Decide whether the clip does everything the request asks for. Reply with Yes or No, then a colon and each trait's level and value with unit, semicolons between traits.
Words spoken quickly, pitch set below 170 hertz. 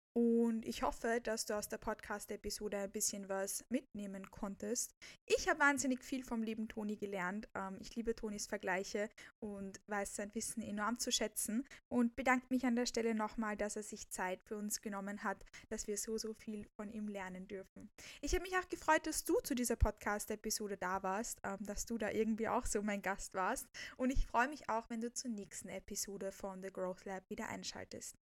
No: fast, 195 wpm; high, 215 Hz